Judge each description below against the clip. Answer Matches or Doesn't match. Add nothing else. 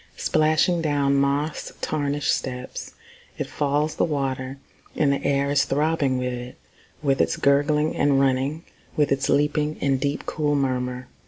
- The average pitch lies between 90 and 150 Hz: Matches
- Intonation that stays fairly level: Matches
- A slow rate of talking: Doesn't match